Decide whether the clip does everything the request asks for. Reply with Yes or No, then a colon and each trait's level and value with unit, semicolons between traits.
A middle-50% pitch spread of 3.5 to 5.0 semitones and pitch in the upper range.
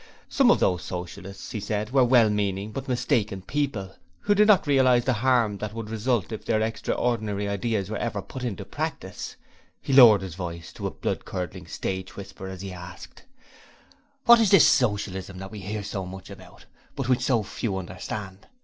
No: average, 4.4 semitones; low, 105 Hz